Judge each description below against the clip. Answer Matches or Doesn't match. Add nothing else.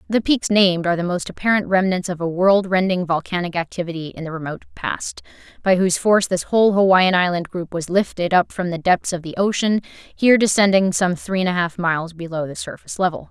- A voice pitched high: Doesn't match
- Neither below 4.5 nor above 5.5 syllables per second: Doesn't match